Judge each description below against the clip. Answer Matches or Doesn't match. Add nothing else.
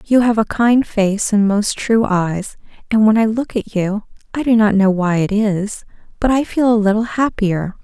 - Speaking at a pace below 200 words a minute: Doesn't match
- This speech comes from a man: Doesn't match